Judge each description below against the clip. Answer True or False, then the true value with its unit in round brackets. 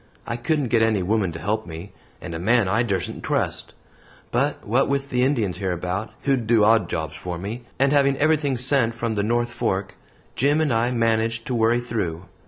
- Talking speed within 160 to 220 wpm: True (195 wpm)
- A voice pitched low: True (115 Hz)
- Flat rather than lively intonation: False (4.3 semitones)